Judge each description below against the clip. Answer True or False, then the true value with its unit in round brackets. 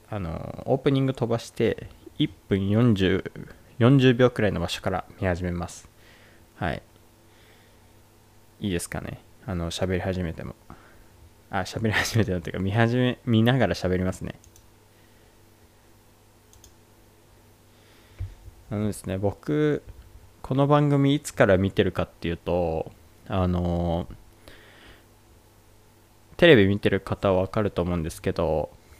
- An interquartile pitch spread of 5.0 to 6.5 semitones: False (3.3 semitones)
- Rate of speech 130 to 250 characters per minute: True (230 characters per minute)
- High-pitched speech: False (105 Hz)